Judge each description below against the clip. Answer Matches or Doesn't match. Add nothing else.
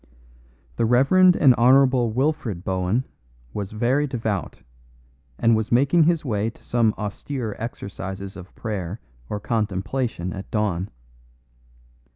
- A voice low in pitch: Matches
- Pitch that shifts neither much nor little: Matches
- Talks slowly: Matches